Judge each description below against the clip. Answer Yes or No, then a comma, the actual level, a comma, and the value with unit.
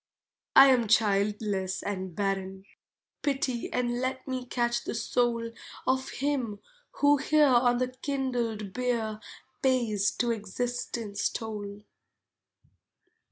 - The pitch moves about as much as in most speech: Yes, average, 3.6 semitones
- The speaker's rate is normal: No, slow, 110 wpm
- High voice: Yes, high, 240 Hz